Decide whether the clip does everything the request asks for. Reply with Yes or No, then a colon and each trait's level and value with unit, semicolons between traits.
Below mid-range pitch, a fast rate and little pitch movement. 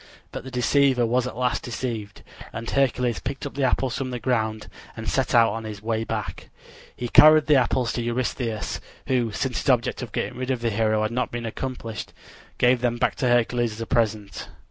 Yes: low, 120 Hz; fast, 210 wpm; narrow, 2.2 semitones